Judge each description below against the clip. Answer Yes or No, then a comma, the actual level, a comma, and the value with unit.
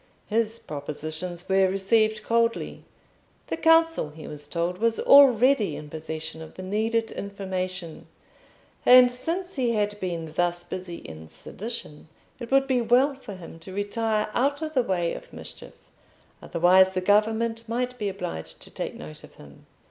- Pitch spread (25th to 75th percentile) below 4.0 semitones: No, average, 5.2 semitones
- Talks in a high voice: Yes, high, 205 Hz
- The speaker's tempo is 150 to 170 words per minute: Yes, average, 155 wpm